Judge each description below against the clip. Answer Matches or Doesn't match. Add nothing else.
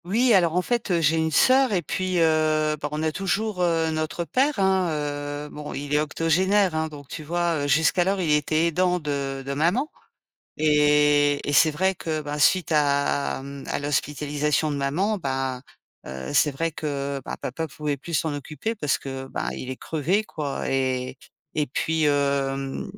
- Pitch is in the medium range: Matches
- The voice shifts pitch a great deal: Doesn't match